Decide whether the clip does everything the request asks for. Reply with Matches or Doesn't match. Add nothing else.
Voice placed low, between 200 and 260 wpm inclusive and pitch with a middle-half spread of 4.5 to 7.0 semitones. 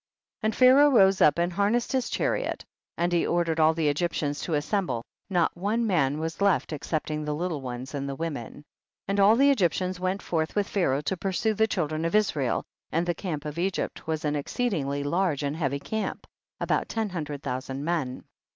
Doesn't match